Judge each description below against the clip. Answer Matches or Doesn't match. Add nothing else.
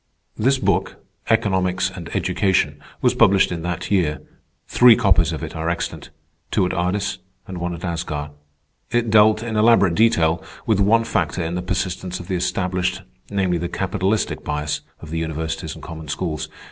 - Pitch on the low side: Matches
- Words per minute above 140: Matches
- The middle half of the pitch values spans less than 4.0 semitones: Matches